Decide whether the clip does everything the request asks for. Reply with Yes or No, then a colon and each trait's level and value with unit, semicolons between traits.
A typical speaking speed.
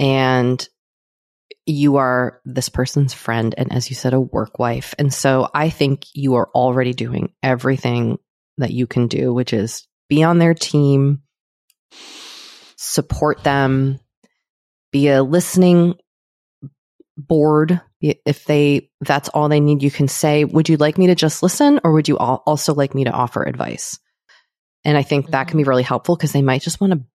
Yes: average, 170 wpm